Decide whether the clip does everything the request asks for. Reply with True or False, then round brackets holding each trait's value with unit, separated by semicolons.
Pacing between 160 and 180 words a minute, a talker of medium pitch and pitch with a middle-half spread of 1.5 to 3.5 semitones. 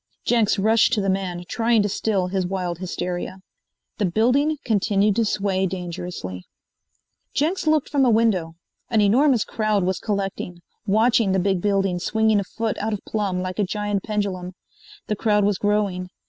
False (165 wpm; 205 Hz; 3.0 semitones)